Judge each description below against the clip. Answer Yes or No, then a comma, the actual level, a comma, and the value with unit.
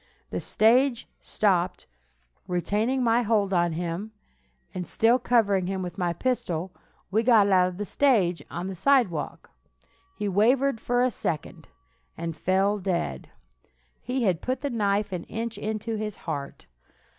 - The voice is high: Yes, high, 205 Hz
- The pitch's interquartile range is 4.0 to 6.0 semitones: Yes, average, 4.5 semitones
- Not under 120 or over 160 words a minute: Yes, average, 145 wpm